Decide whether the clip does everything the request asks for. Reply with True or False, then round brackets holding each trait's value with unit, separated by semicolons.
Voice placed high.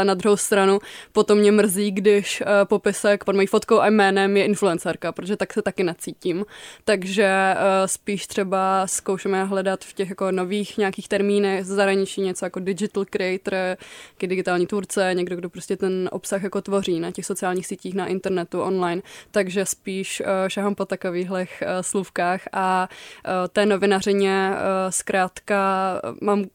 True (195 Hz)